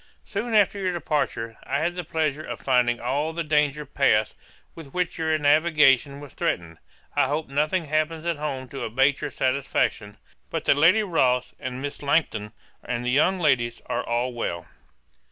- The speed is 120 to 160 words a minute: No, average, 170 wpm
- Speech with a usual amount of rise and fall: Yes, average, 4.1 semitones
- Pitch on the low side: No, medium, 145 Hz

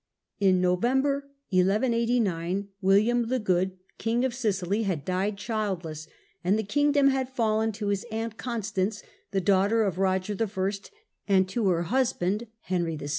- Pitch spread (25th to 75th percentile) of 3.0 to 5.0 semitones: Yes, average, 3.7 semitones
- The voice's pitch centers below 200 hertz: No, high, 205 Hz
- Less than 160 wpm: Yes, average, 145 wpm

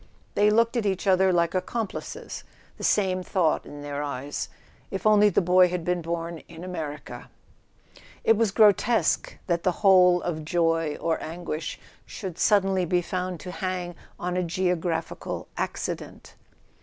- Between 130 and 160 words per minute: Yes, average, 155 wpm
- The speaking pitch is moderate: Yes, medium, 180 Hz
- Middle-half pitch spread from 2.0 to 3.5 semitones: Yes, narrow, 2.5 semitones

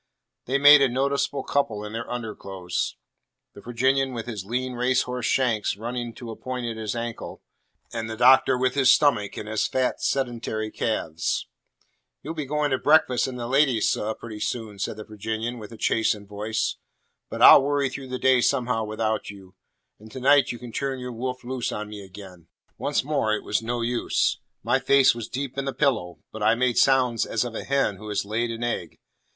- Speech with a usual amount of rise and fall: Yes, average, 3.2 semitones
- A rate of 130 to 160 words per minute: No, average, 200 wpm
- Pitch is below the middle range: Yes, low, 120 Hz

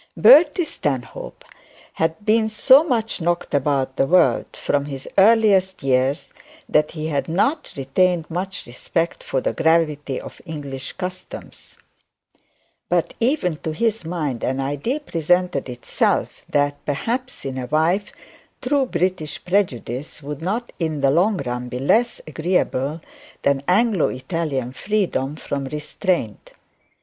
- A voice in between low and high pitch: Yes, medium, 160 Hz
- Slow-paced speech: Yes, slow, 130 wpm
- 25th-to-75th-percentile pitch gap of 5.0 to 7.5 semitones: Yes, wide, 5.6 semitones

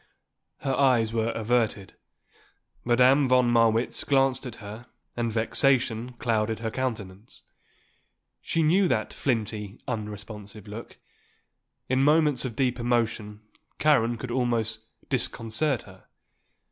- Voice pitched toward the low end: Yes, low, 120 Hz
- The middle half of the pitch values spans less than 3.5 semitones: Yes, average, 2.9 semitones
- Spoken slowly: Yes, slow, 110 wpm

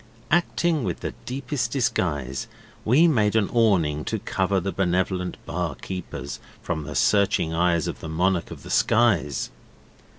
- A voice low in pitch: Yes, very low, 95 Hz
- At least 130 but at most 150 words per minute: Yes, average, 145 wpm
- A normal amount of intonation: No, wide, 5.8 semitones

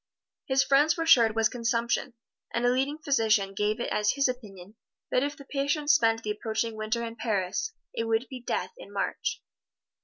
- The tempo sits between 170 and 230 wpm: Yes, average, 190 wpm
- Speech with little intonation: No, average, 3.9 semitones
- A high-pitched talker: Yes, high, 235 Hz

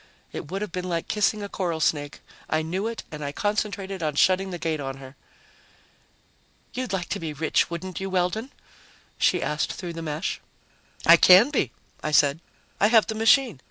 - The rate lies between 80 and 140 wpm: No, average, 190 wpm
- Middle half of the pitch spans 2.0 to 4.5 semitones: No, average, 4.9 semitones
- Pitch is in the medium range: Yes, medium, 180 Hz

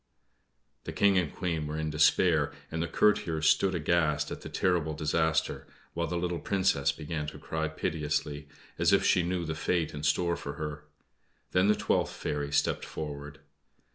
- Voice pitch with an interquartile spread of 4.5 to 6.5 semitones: No, narrow, 2.6 semitones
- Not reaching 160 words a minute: No, average, 170 wpm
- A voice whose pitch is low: Yes, very low, 80 Hz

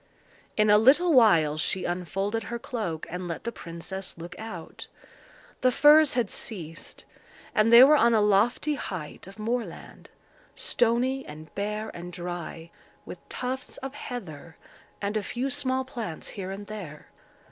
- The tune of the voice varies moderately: No, wide, 5.8 semitones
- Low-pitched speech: No, high, 210 Hz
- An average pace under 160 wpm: Yes, average, 150 wpm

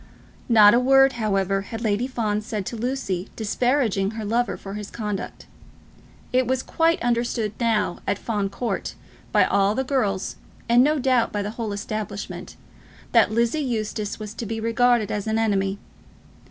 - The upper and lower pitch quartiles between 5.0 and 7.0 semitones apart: No, average, 2.9 semitones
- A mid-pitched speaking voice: No, high, 220 Hz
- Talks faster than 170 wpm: No, average, 165 wpm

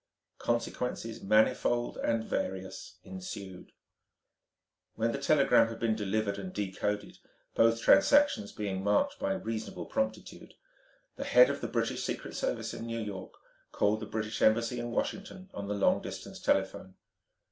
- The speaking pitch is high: No, low, 110 Hz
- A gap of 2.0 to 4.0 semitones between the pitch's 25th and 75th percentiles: Yes, average, 2.9 semitones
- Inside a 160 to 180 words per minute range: No, average, 140 wpm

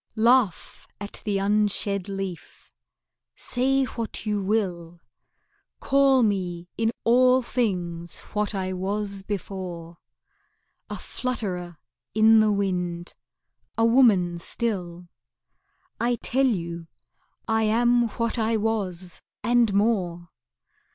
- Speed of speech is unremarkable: No, slow, 105 wpm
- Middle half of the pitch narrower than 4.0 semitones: No, average, 4.4 semitones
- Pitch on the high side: Yes, high, 205 Hz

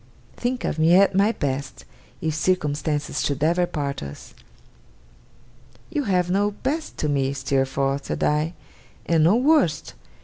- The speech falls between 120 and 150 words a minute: Yes, average, 140 wpm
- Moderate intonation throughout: No, wide, 5.7 semitones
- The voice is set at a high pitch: No, medium, 160 Hz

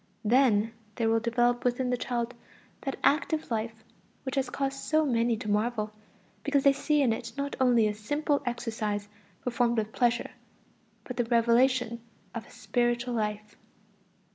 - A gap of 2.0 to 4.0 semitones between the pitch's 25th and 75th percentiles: Yes, narrow, 2.5 semitones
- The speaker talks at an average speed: Yes, average, 155 wpm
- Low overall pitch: No, high, 240 Hz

